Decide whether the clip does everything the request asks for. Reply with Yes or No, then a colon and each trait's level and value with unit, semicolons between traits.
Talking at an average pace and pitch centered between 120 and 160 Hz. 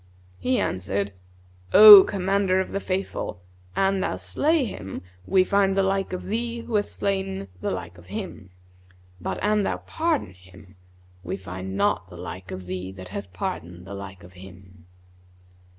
No: average, 165 wpm; low, 100 Hz